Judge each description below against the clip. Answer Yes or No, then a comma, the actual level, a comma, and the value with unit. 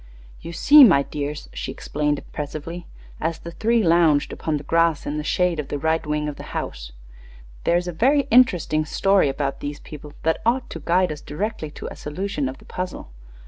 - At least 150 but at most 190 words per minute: No, average, 200 wpm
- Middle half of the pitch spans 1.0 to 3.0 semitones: No, average, 3.4 semitones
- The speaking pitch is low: No, medium, 160 Hz